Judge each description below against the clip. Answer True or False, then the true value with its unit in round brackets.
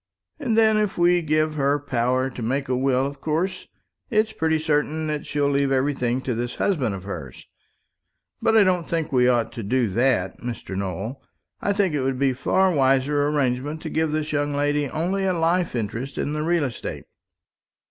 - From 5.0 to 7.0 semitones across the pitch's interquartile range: False (4.1 semitones)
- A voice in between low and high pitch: True (145 Hz)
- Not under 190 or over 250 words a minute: True (195 wpm)